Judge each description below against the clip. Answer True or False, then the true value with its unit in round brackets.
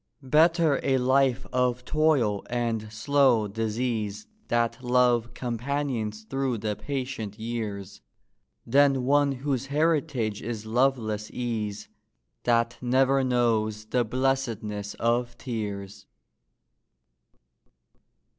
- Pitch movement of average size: True (3.6 semitones)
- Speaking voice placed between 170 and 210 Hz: False (120 Hz)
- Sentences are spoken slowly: True (95 wpm)